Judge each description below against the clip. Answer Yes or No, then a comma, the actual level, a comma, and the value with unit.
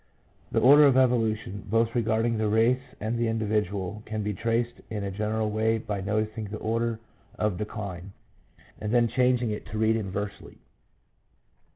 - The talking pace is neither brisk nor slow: Yes, average, 160 wpm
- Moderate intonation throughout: No, narrow, 1.7 semitones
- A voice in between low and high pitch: No, low, 110 Hz